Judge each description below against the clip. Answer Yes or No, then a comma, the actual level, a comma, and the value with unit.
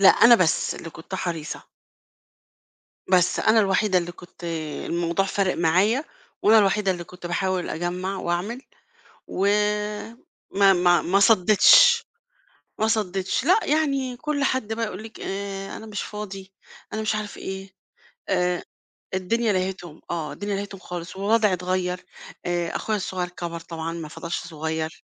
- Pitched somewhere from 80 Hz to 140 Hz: No, high, 190 Hz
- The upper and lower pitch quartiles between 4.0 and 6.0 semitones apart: No, average, 3.3 semitones